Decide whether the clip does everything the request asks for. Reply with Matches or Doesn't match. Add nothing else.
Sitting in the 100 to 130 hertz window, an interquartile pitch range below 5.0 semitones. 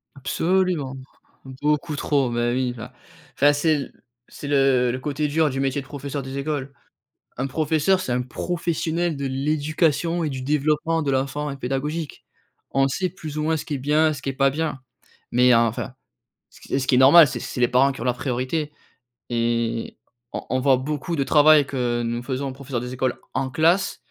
Doesn't match